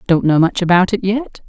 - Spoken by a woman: Yes, female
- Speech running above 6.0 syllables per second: No, 5.3 syllables/s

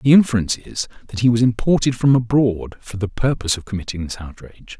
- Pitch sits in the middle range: No, low, 110 Hz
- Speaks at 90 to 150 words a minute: No, average, 200 wpm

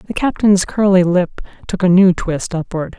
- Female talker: Yes, female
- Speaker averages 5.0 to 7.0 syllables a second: No, 4.5 syllables/s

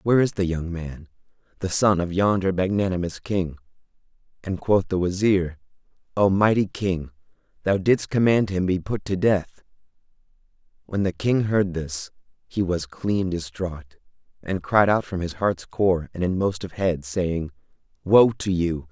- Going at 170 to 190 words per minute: No, average, 160 wpm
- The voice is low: Yes, very low, 95 Hz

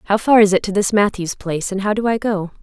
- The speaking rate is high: Yes, fast, 300 wpm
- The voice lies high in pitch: Yes, high, 200 Hz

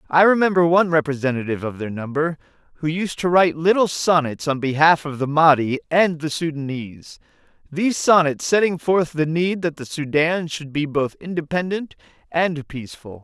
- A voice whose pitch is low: No, medium, 155 Hz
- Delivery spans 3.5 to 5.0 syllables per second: No, 5.3 syllables/s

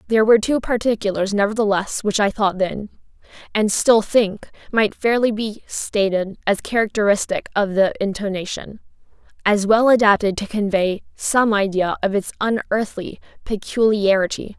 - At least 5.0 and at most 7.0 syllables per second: No, 4.8 syllables/s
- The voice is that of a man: No, female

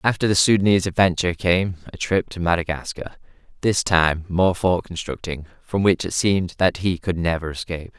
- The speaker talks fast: No, average, 165 wpm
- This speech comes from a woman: No, male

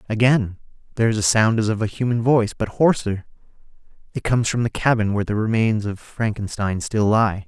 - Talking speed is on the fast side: No, average, 195 wpm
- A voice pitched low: Yes, low, 110 Hz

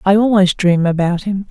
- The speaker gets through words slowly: No, average, 200 wpm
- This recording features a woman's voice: Yes, female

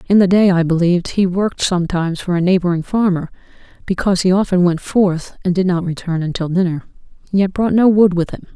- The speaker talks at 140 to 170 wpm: No, fast, 205 wpm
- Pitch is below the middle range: No, medium, 180 Hz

